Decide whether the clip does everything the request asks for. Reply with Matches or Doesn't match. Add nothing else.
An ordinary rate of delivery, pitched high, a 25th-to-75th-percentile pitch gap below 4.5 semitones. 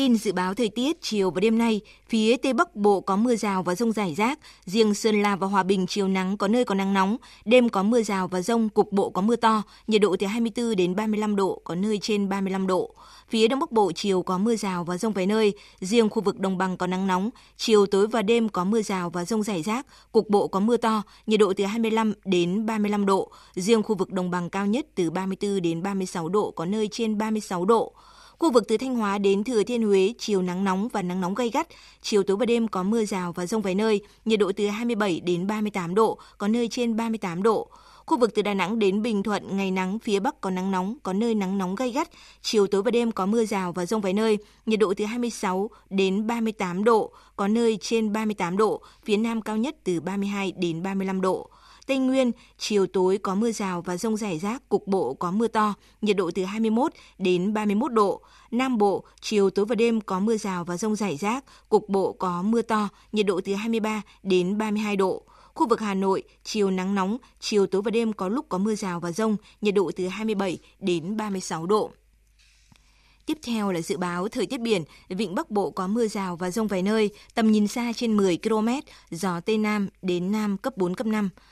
Matches